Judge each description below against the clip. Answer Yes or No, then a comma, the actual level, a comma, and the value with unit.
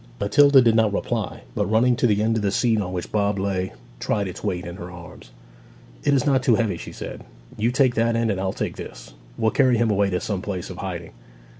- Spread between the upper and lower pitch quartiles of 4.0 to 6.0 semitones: No, average, 3.6 semitones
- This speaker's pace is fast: Yes, fast, 240 wpm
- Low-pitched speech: Yes, low, 105 Hz